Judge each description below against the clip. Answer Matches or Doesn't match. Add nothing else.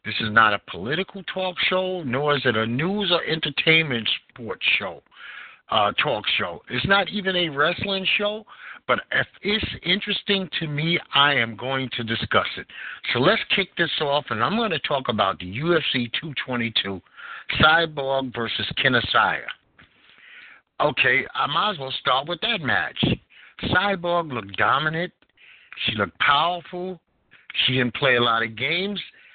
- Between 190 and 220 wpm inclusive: Doesn't match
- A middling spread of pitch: Doesn't match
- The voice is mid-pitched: Matches